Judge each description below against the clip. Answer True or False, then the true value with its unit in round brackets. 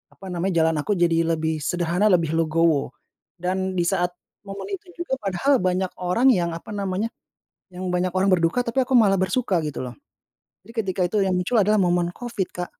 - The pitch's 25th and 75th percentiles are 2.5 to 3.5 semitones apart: True (3.1 semitones)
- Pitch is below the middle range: False (185 Hz)